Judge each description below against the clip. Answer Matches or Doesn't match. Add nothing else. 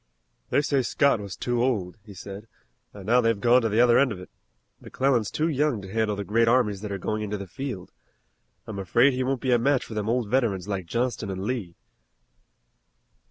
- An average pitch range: Matches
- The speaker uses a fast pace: Matches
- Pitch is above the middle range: Doesn't match